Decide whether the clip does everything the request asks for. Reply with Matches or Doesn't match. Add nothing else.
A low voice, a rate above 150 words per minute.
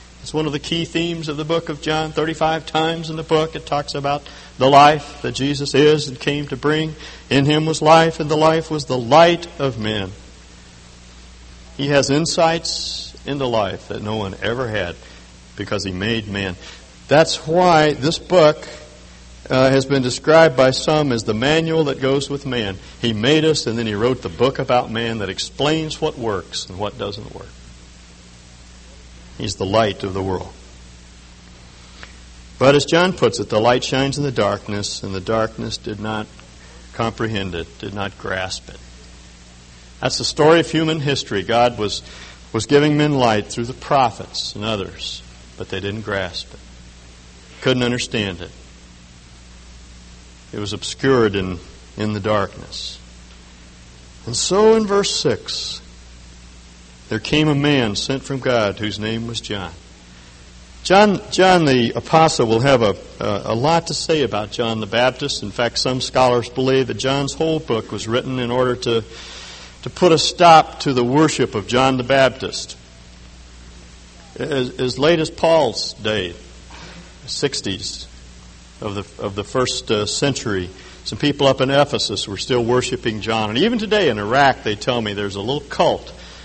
Matches